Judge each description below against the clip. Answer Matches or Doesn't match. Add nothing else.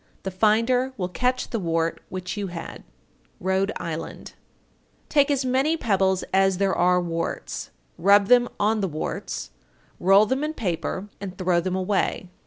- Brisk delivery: Doesn't match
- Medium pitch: Doesn't match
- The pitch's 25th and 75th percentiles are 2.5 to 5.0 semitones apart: Matches